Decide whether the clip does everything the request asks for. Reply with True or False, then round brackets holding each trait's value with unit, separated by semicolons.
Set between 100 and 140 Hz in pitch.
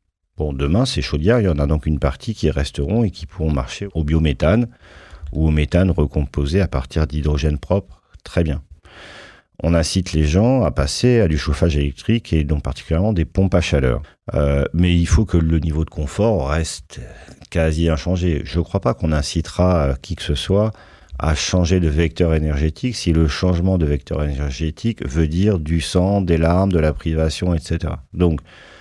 False (80 Hz)